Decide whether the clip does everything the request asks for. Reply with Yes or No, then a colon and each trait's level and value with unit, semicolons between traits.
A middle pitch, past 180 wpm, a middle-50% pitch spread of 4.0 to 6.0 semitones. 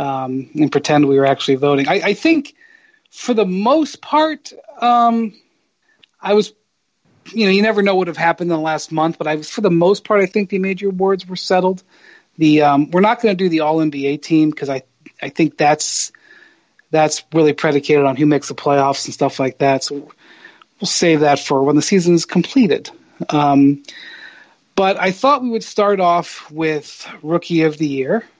Yes: medium, 165 Hz; average, 200 wpm; wide, 5.6 semitones